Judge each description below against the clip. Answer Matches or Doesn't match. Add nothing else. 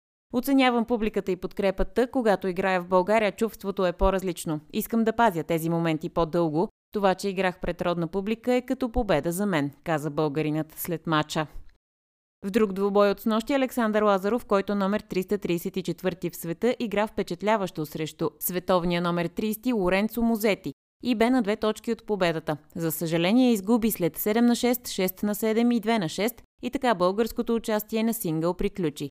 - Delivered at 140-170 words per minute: Matches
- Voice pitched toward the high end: Matches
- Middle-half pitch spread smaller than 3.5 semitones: Doesn't match